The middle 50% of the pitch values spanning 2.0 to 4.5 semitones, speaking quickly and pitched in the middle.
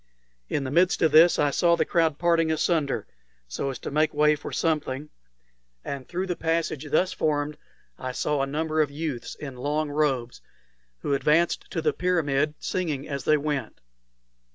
No: narrow, 2.6 semitones; average, 175 wpm; medium, 150 Hz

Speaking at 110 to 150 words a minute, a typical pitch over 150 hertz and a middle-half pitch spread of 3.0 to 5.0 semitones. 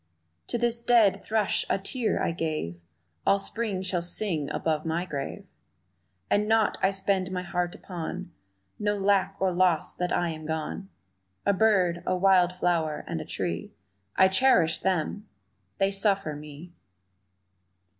Yes: average, 145 wpm; medium, 185 Hz; average, 3.4 semitones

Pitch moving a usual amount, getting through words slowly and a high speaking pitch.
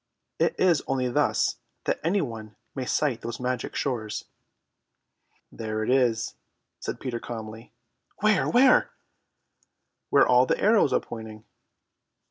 No: average, 4.2 semitones; slow, 125 wpm; low, 125 Hz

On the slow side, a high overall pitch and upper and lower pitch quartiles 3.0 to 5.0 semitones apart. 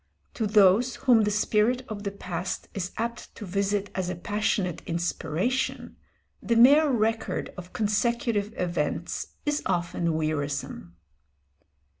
Yes: slow, 125 wpm; high, 205 Hz; average, 4.6 semitones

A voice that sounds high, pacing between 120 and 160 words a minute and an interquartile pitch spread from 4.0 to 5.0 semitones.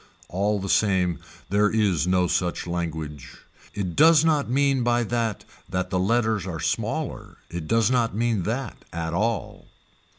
No: low, 105 Hz; average, 155 wpm; average, 4.7 semitones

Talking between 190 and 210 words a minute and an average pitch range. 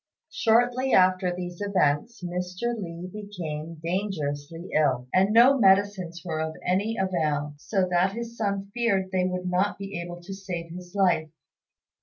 No: average, 150 wpm; average, 3.1 semitones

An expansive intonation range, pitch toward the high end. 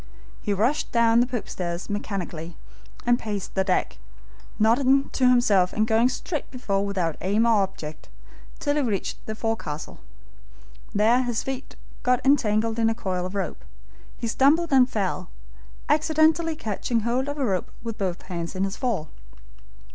No: average, 4.5 semitones; high, 225 Hz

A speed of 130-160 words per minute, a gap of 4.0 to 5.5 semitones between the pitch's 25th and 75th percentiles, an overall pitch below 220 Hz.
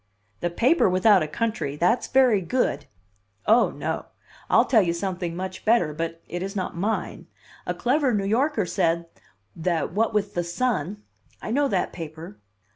No: average, 170 wpm; average, 5.1 semitones; high, 190 Hz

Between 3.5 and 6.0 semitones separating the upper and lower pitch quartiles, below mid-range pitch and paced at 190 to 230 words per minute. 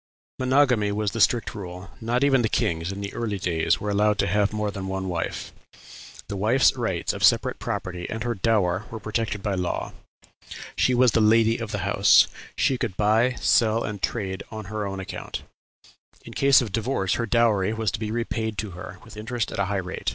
No: average, 3.0 semitones; low, 105 Hz; fast, 205 wpm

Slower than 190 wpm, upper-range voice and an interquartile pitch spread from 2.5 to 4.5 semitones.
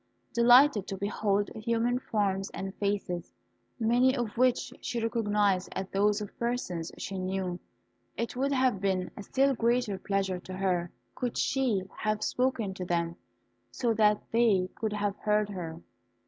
Yes: average, 150 wpm; high, 210 Hz; average, 3.6 semitones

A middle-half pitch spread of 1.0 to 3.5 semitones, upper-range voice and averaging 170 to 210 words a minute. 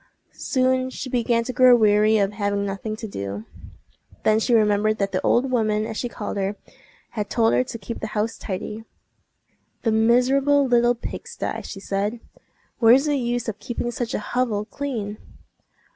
Yes: average, 2.8 semitones; high, 225 Hz; average, 175 wpm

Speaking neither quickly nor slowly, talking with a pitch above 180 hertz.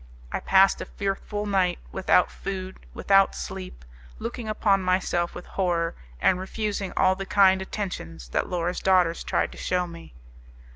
Yes: average, 150 wpm; high, 190 Hz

